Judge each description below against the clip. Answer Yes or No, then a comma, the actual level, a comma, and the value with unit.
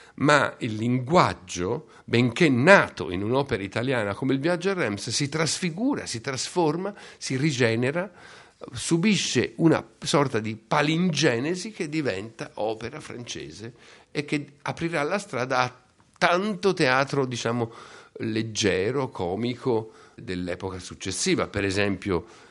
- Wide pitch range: Yes, wide, 6.5 semitones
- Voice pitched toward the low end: Yes, low, 130 Hz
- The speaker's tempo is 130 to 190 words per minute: No, slow, 115 wpm